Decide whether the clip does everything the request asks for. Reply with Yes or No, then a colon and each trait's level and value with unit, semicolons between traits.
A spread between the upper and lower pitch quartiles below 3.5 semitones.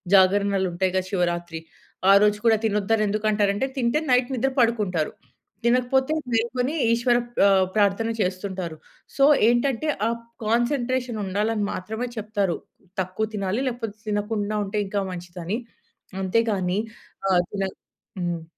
No: average, 3.9 semitones